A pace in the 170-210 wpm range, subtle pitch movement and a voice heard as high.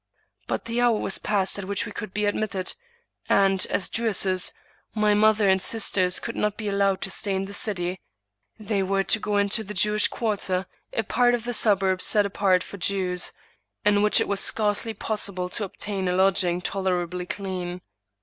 Yes: average, 185 wpm; narrow, 2.1 semitones; high, 200 Hz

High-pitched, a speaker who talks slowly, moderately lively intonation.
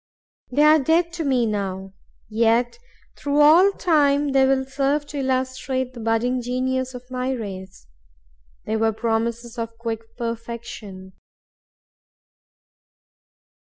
Yes: very high, 250 Hz; slow, 115 wpm; average, 3.3 semitones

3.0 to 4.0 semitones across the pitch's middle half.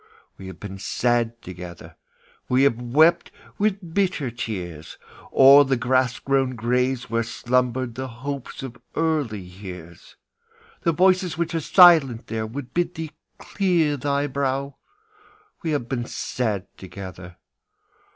No: average, 4.5 semitones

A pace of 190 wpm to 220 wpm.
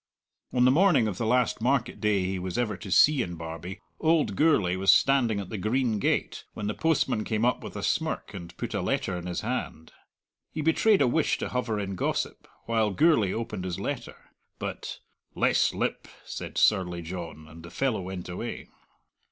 Yes: average, 195 wpm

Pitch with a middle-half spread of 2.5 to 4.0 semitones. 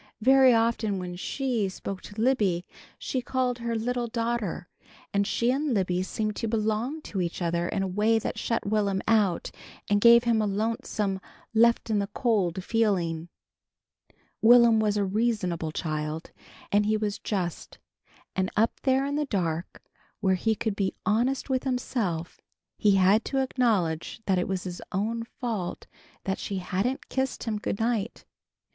Yes: average, 3.7 semitones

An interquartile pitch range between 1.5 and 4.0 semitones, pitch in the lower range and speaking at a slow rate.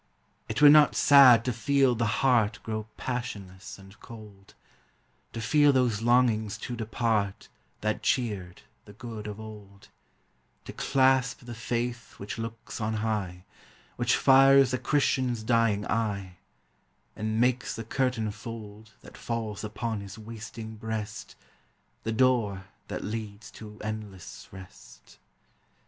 Yes: average, 2.7 semitones; low, 110 Hz; slow, 130 wpm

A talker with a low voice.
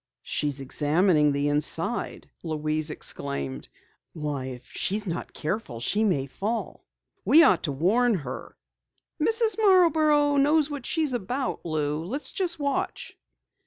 No: medium, 185 Hz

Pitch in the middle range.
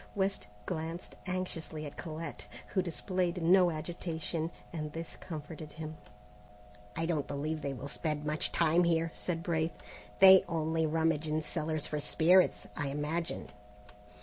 Yes: medium, 160 Hz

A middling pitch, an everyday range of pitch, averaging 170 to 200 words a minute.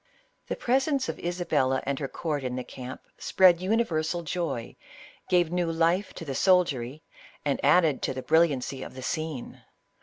No: medium, 160 Hz; average, 4.8 semitones; average, 160 wpm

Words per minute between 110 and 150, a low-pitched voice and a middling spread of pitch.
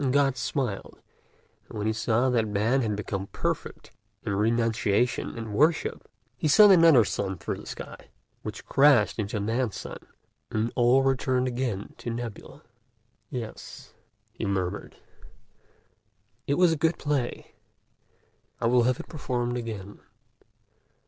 Yes: slow, 135 wpm; low, 120 Hz; average, 3.7 semitones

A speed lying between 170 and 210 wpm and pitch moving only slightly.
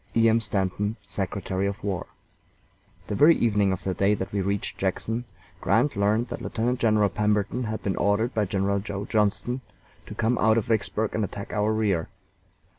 Yes: average, 180 wpm; narrow, 2.1 semitones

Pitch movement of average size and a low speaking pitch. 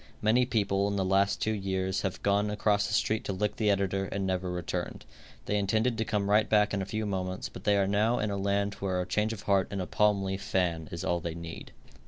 No: narrow, 1.7 semitones; low, 100 Hz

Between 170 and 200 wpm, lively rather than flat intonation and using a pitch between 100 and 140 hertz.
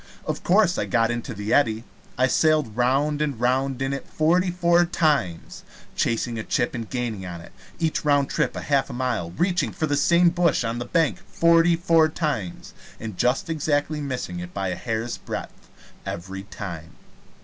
Yes: average, 180 wpm; wide, 5.9 semitones; low, 135 Hz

